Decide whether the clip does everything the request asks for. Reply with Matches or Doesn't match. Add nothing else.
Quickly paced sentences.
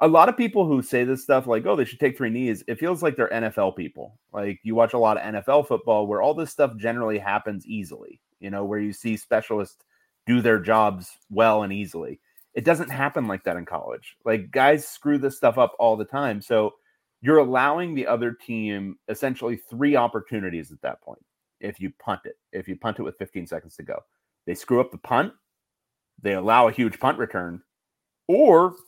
Matches